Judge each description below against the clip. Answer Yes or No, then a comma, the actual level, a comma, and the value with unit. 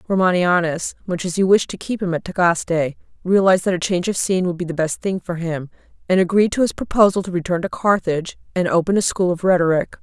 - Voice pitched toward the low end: No, medium, 180 Hz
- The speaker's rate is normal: No, fast, 225 wpm